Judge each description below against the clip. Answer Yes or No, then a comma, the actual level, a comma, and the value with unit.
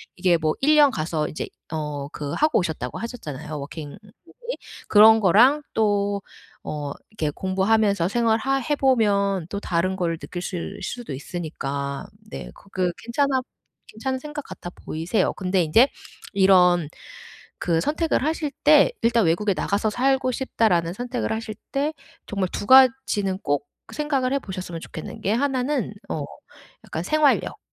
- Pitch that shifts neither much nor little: No, wide, 7.4 semitones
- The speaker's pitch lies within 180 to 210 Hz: Yes, high, 200 Hz